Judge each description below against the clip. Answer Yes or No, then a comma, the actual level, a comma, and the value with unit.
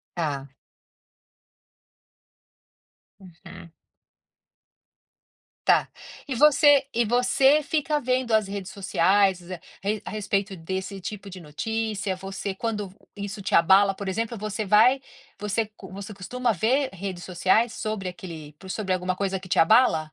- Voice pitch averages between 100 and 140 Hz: No, high, 200 Hz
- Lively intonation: No, average, 3.1 semitones